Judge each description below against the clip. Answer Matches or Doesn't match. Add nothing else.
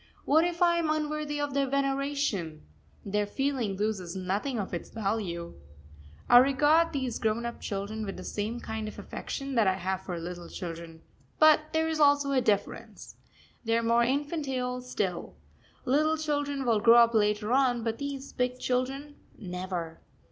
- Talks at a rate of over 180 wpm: Doesn't match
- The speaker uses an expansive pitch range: Matches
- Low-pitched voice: Doesn't match